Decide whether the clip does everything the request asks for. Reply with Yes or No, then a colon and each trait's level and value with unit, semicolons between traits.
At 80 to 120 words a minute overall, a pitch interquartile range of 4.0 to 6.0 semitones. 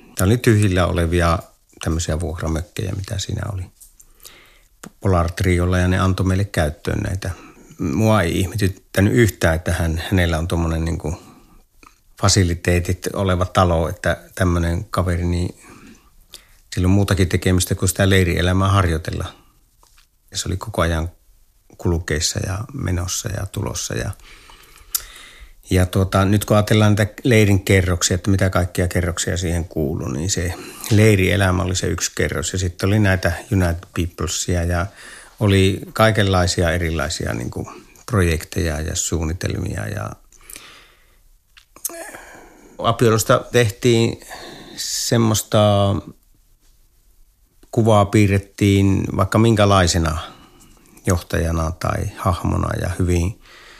No: average, 115 wpm; average, 2.8 semitones